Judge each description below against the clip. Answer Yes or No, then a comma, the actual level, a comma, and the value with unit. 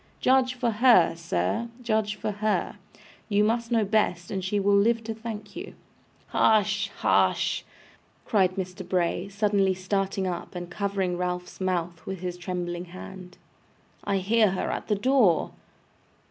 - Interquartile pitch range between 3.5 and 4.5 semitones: No, average, 3.1 semitones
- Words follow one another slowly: No, average, 145 wpm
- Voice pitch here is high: Yes, high, 195 Hz